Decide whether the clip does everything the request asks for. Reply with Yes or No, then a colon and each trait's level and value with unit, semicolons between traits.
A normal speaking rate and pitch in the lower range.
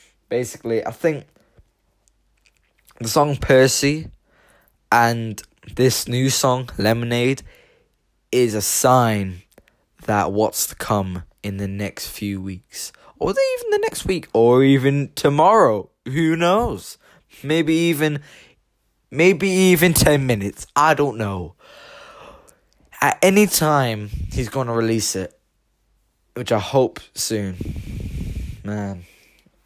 No: slow, 110 wpm; low, 120 Hz